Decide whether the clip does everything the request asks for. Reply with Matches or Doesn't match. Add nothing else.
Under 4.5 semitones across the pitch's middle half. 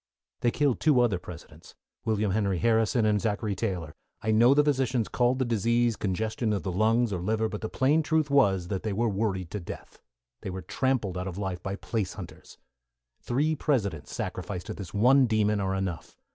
Matches